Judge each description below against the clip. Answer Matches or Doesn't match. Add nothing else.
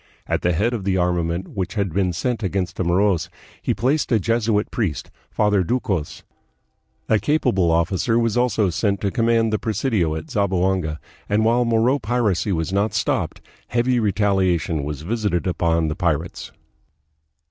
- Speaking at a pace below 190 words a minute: Matches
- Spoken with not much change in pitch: Doesn't match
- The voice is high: Doesn't match